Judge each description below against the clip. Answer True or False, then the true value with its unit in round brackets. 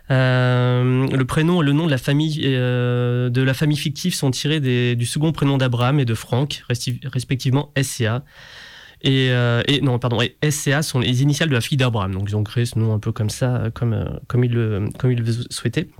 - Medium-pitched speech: False (130 Hz)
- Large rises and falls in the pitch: False (2.7 semitones)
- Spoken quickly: True (225 wpm)